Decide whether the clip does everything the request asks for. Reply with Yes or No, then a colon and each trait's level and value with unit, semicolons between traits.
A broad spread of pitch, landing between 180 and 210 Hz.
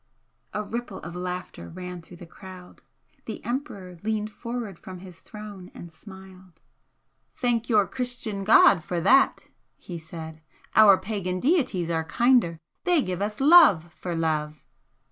No: average, 4.2 semitones; high, 190 Hz